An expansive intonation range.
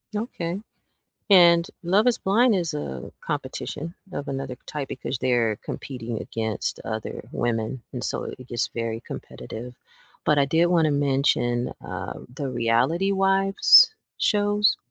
Yes: wide, 7.6 semitones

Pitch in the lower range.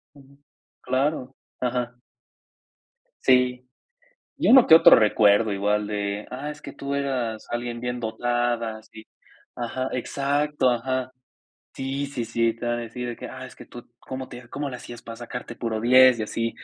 Yes: low, 125 Hz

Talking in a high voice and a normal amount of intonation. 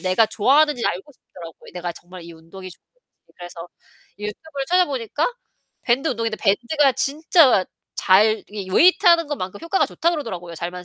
No: high, 225 Hz; wide, 8.2 semitones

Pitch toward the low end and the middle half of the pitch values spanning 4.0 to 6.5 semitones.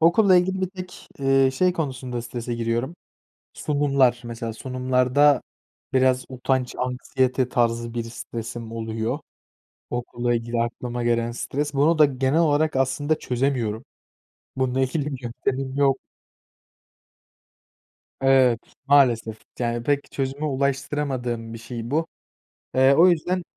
No: low, 130 Hz; average, 3.1 semitones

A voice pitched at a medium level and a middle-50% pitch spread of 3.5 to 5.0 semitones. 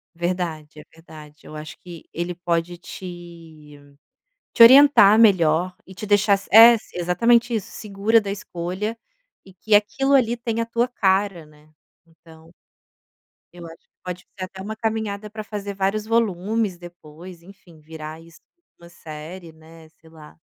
Yes: medium, 180 Hz; average, 4.5 semitones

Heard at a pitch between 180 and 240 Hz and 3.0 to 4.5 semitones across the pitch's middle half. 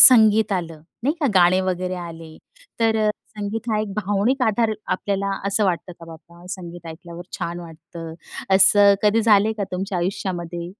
Yes: medium, 185 Hz; average, 3.5 semitones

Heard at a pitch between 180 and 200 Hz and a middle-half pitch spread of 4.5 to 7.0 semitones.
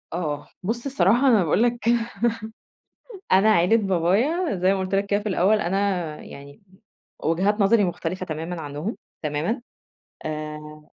Yes: medium, 185 Hz; average, 5.0 semitones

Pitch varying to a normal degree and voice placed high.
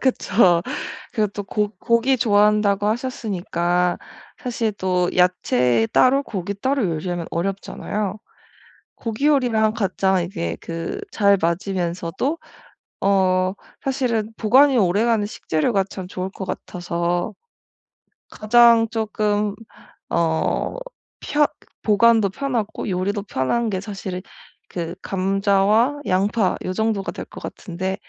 Yes: average, 3.7 semitones; high, 200 Hz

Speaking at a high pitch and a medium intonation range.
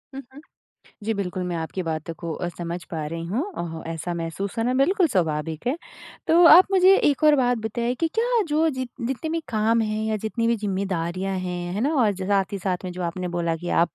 No: high, 200 Hz; wide, 6.7 semitones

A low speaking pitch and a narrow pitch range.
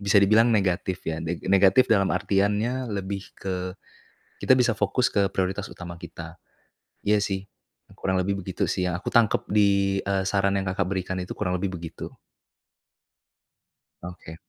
Yes: very low, 95 Hz; narrow, 1.9 semitones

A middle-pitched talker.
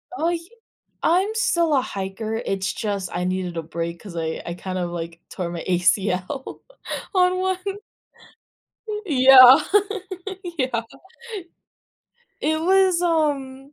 No: high, 235 Hz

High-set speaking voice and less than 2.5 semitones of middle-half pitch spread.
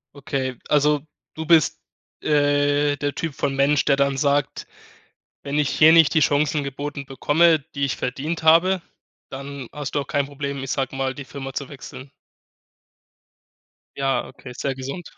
No: medium, 140 Hz; narrow, 1.5 semitones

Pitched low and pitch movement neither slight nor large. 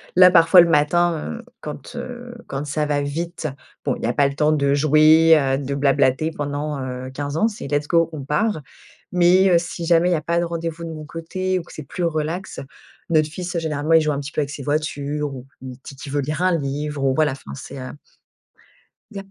No: medium, 155 Hz; average, 3.0 semitones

